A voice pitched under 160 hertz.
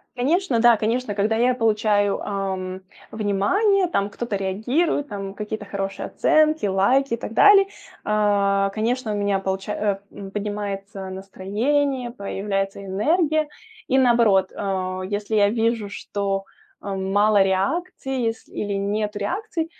No: high, 210 Hz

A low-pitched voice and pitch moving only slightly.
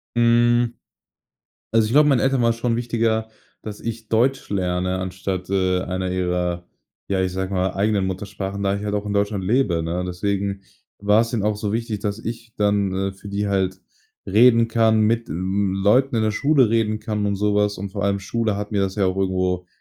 No: low, 100 Hz; average, 3.1 semitones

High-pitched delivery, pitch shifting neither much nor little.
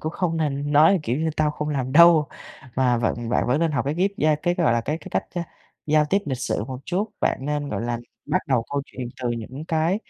No: medium, 150 Hz; average, 4.1 semitones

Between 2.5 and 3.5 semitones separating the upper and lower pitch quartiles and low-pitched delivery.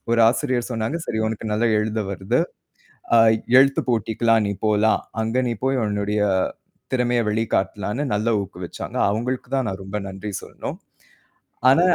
Yes: average, 2.9 semitones; low, 110 Hz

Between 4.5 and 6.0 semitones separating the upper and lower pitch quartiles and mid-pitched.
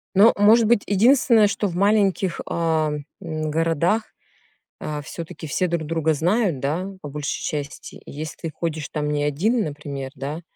Yes: average, 5.1 semitones; medium, 165 Hz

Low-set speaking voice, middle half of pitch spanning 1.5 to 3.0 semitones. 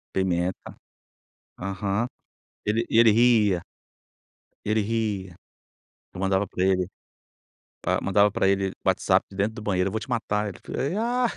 Yes: low, 100 Hz; narrow, 2.5 semitones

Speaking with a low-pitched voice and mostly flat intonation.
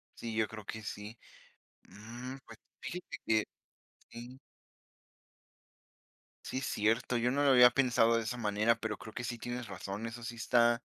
Yes: low, 115 Hz; narrow, 1.9 semitones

